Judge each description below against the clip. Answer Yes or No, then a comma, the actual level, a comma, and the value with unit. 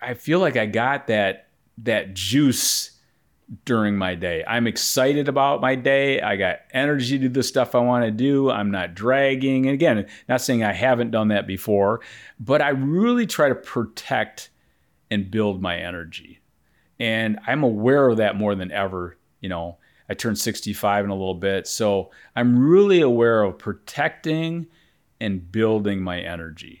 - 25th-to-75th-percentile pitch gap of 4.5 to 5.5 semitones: Yes, average, 5.2 semitones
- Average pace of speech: Yes, average, 170 wpm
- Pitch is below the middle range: Yes, low, 115 Hz